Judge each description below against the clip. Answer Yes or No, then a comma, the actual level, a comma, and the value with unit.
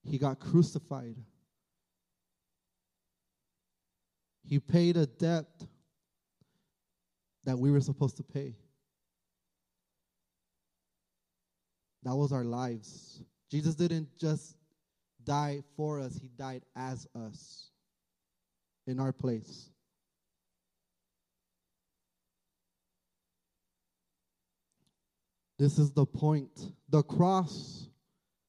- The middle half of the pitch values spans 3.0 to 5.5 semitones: Yes, average, 3.5 semitones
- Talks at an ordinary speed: No, slow, 75 wpm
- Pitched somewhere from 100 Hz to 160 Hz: Yes, medium, 140 Hz